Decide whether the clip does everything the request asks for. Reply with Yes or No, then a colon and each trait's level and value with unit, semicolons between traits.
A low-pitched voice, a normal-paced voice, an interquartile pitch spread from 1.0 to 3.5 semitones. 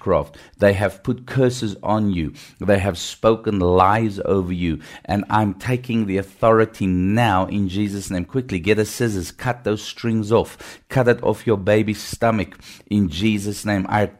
Yes: low, 105 Hz; average, 170 wpm; narrow, 2.5 semitones